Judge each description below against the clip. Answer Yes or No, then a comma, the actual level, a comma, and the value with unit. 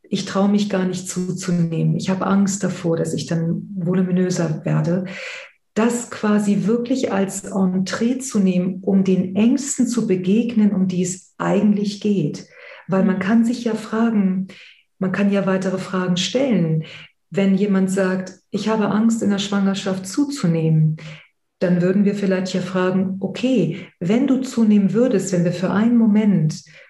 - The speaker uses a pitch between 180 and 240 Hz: Yes, high, 190 Hz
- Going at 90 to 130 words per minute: No, average, 155 wpm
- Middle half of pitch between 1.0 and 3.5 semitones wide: Yes, narrow, 2.4 semitones